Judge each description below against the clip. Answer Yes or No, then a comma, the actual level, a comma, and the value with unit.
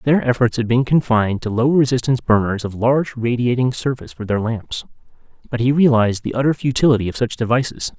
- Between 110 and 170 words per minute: No, average, 190 wpm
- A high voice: No, low, 120 Hz